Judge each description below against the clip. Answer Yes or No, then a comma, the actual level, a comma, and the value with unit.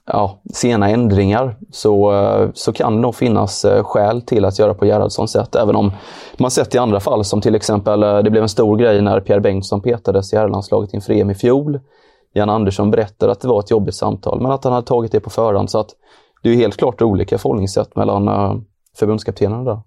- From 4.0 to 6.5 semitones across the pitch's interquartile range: No, narrow, 2.5 semitones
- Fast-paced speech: Yes, fast, 210 wpm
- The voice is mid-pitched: No, low, 105 Hz